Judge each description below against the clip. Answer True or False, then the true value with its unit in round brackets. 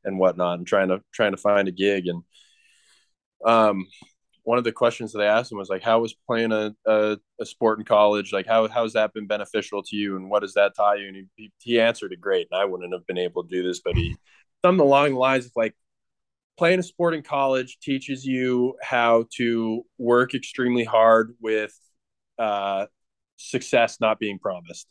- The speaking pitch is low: True (110 Hz)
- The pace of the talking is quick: True (210 wpm)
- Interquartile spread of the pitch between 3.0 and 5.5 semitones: True (3.5 semitones)